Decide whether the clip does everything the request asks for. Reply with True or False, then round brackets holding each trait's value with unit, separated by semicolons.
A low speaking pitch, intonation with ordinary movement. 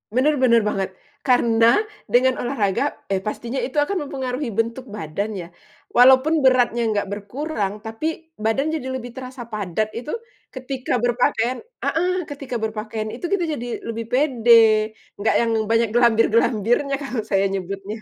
False (240 Hz; 3.3 semitones)